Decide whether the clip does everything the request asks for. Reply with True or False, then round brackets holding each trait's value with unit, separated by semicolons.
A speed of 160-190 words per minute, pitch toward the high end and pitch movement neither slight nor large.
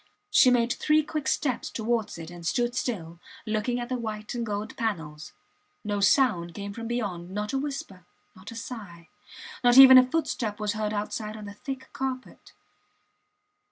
True (170 wpm; 220 Hz; 3.6 semitones)